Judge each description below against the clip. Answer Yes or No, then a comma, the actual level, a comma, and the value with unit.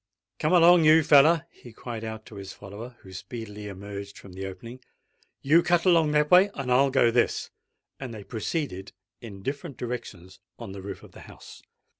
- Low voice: Yes, low, 120 Hz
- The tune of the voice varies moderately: No, wide, 6.8 semitones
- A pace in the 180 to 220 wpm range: Yes, average, 185 wpm